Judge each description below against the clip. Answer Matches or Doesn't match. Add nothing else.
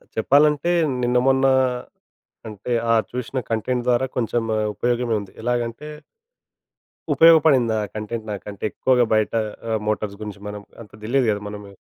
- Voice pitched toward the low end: Matches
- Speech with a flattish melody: Doesn't match